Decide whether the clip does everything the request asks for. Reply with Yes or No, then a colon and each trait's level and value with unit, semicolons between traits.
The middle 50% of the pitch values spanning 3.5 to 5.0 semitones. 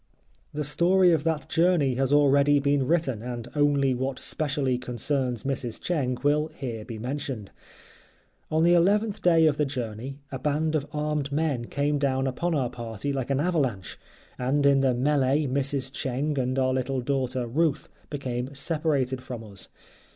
No: average, 2.8 semitones